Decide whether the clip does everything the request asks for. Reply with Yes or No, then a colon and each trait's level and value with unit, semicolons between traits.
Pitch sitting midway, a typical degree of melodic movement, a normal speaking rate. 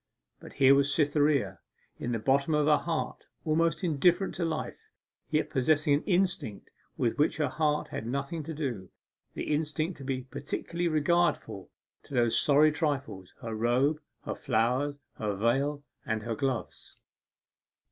Yes: medium, 145 Hz; average, 3.8 semitones; average, 150 wpm